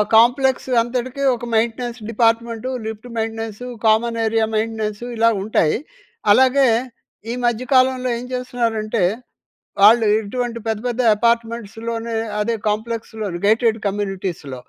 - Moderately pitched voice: No, high, 230 Hz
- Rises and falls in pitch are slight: Yes, narrow, 1.6 semitones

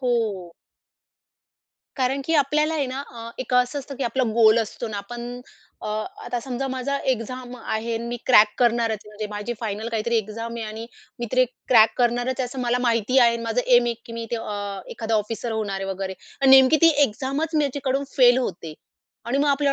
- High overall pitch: Yes, high, 240 Hz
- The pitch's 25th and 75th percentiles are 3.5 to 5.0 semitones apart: No, average, 2.9 semitones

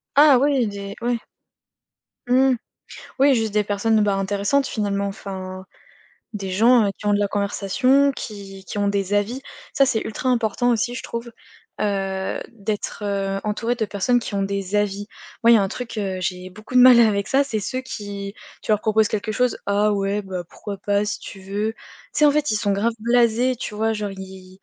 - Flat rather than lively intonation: No, average, 3.0 semitones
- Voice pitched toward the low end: No, high, 210 Hz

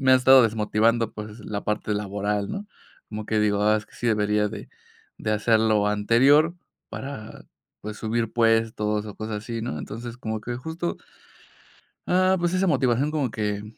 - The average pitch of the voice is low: Yes, low, 110 Hz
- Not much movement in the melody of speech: No, average, 3.1 semitones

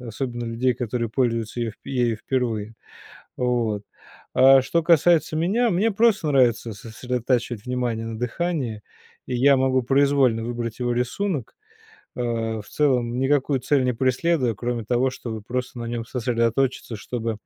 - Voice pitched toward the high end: No, low, 125 Hz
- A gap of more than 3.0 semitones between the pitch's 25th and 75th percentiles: No, average, 2.7 semitones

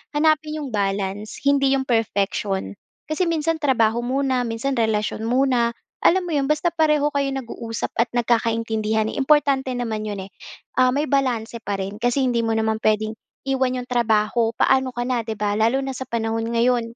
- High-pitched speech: Yes, high, 240 Hz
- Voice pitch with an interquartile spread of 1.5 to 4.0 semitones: Yes, average, 3.6 semitones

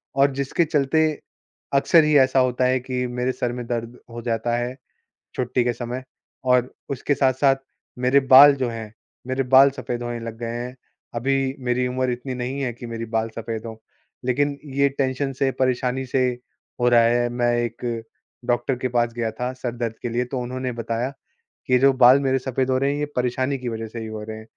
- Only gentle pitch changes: Yes, narrow, 1.8 semitones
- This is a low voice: Yes, low, 125 Hz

